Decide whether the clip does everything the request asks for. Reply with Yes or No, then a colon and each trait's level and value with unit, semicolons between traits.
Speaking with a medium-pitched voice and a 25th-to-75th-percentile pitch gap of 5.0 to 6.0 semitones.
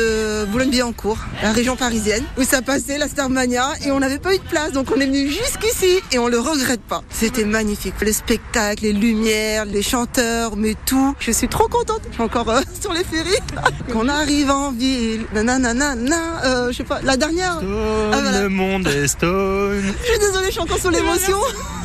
No: very high, 255 Hz; average, 5.3 semitones